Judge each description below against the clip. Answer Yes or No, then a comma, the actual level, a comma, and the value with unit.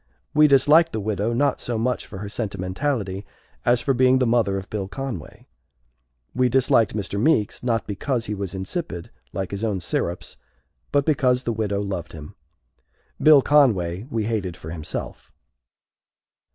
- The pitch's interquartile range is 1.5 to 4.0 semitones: No, average, 4.9 semitones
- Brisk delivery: No, average, 155 wpm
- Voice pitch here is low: Yes, low, 110 Hz